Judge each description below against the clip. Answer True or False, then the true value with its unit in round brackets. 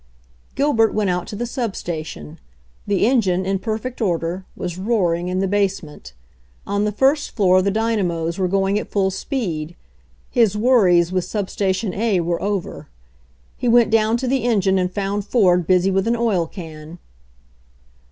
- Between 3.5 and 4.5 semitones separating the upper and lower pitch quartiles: True (3.9 semitones)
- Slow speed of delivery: False (170 wpm)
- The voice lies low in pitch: False (195 Hz)